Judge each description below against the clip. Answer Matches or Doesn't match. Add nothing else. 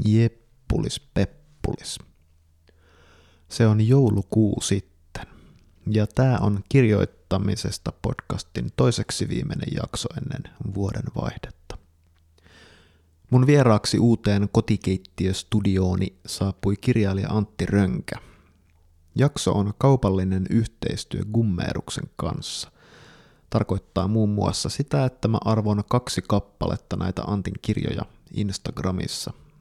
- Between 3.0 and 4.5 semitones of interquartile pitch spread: Matches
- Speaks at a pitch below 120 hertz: Matches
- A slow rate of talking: Matches